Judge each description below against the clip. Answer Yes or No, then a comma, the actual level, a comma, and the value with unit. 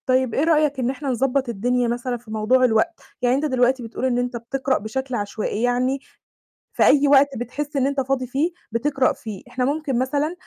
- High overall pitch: Yes, very high, 255 Hz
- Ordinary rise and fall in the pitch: No, narrow, 2.2 semitones